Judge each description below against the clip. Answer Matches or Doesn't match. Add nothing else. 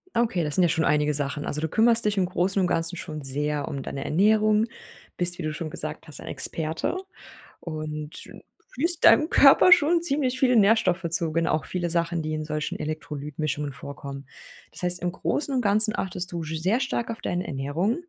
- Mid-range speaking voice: Matches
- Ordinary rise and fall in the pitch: Doesn't match